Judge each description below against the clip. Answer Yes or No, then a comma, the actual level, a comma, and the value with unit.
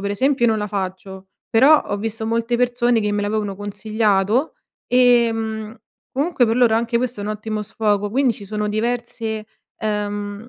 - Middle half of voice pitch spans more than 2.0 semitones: Yes, narrow, 2.5 semitones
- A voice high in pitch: Yes, high, 220 Hz